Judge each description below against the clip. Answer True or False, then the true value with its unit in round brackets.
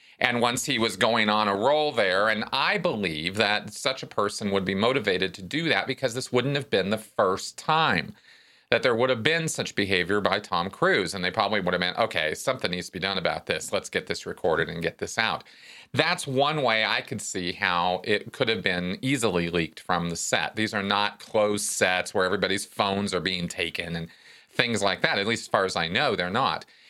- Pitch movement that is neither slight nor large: False (6.0 semitones)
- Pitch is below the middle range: True (105 Hz)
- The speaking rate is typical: False (230 wpm)